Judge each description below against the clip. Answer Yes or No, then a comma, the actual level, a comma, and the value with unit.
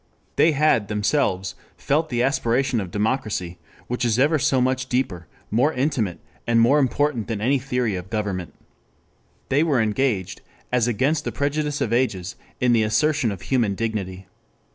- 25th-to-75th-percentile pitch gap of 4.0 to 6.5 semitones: Yes, average, 4.7 semitones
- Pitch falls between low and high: No, low, 120 Hz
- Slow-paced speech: No, average, 160 wpm